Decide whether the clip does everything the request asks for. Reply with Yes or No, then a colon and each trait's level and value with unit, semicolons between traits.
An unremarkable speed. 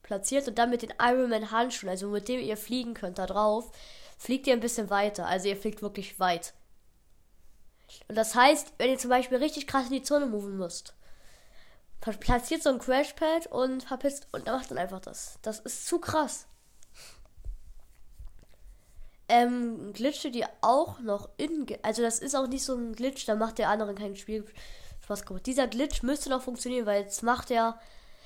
Yes: average, 180 wpm